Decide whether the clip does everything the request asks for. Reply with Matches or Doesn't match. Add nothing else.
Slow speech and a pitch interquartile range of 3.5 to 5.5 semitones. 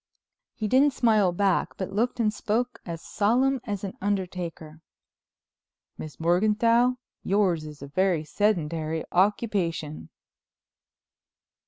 Matches